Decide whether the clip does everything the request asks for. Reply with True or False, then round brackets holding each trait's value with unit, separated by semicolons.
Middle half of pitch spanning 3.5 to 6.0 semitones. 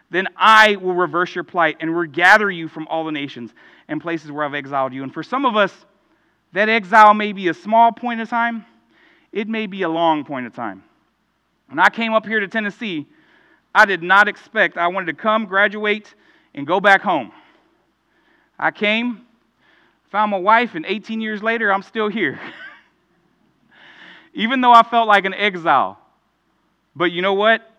True (4.5 semitones)